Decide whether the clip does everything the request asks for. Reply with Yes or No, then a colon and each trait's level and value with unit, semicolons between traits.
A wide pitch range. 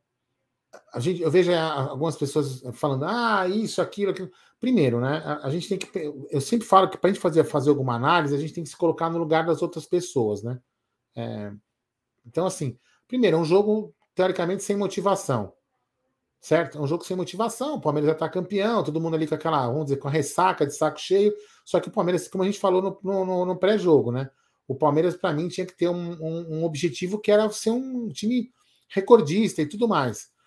No: average, 4.7 semitones